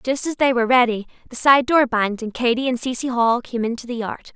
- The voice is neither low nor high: No, high, 245 Hz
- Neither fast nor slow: No, fast, 250 wpm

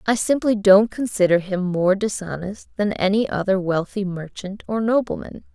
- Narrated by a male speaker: No, female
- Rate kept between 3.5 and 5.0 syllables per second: Yes, 4.8 syllables/s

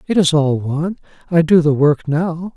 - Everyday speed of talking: Yes, average, 190 wpm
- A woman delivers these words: No, male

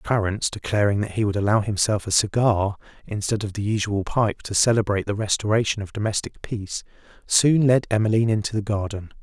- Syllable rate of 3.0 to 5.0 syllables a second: No, 5.9 syllables/s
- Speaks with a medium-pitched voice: No, low, 105 Hz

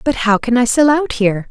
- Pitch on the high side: Yes, high, 245 Hz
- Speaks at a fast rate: Yes, fast, 280 wpm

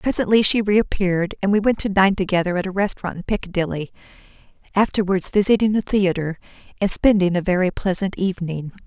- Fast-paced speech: No, average, 160 wpm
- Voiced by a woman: Yes, female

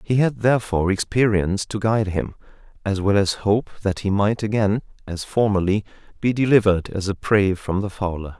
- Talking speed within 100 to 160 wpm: No, average, 180 wpm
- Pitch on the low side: Yes, low, 105 Hz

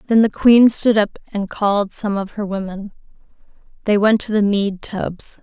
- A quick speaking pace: No, average, 190 wpm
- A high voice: Yes, high, 205 Hz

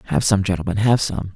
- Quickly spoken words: Yes, fast, 220 wpm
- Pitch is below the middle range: Yes, low, 100 Hz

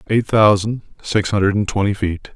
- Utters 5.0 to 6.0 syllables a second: No, 4.5 syllables/s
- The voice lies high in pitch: No, low, 105 Hz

